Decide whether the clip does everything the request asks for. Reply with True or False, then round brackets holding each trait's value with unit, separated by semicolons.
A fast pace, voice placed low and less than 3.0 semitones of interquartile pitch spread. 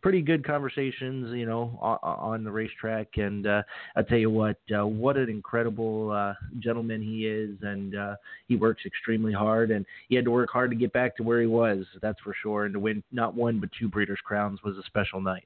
True (220 wpm; 110 Hz; 2.4 semitones)